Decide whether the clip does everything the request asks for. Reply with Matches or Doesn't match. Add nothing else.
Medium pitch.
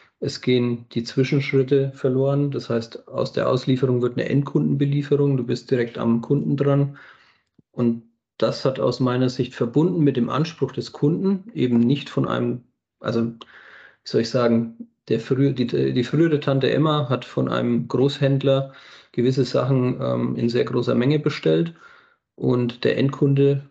Doesn't match